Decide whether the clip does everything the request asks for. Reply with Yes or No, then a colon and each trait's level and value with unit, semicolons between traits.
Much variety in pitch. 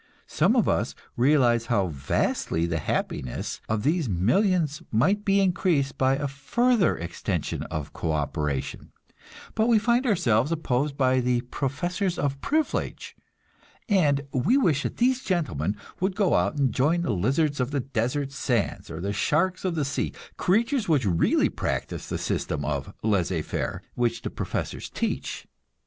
Yes: wide, 8.3 semitones